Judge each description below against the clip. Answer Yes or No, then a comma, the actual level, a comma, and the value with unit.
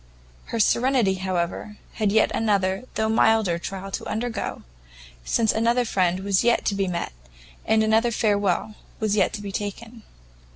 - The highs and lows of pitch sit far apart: No, average, 2.7 semitones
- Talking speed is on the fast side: No, average, 155 wpm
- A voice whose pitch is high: Yes, high, 210 Hz